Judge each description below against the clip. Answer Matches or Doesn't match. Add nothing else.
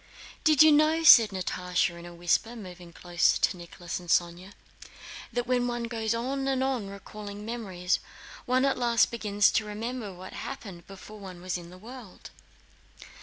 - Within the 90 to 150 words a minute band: Doesn't match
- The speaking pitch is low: Doesn't match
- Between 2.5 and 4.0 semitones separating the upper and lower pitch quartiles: Doesn't match